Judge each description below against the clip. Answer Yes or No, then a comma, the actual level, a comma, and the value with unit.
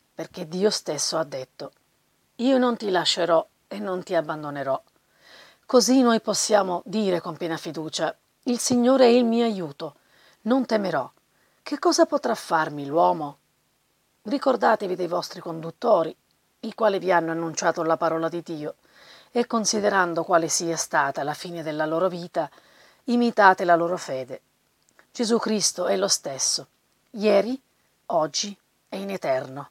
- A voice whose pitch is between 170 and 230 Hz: Yes, medium, 185 Hz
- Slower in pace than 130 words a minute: No, average, 140 wpm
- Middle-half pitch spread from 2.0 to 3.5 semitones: No, wide, 5.6 semitones